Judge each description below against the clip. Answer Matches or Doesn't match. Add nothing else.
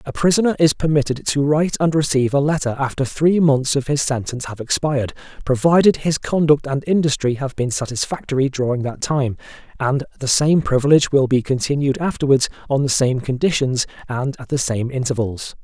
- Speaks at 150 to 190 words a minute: Matches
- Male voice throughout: Matches